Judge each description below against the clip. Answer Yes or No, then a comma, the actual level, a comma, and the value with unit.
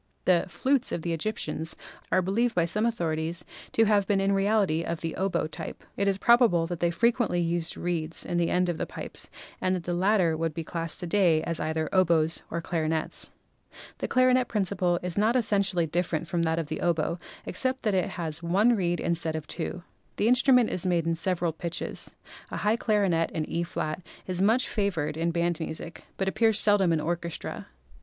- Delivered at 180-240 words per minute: Yes, average, 195 wpm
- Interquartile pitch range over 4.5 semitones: No, average, 3.6 semitones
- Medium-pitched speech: Yes, medium, 175 Hz